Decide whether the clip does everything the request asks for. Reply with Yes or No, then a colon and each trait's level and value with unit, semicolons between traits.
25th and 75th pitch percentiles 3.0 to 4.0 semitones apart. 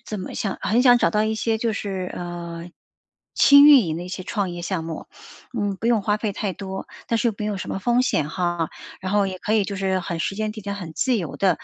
Yes: average, 3.4 semitones